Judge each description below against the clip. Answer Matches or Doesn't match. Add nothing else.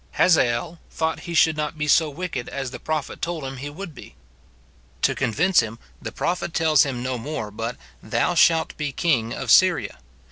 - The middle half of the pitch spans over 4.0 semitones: Matches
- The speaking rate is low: Doesn't match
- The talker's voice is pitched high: Doesn't match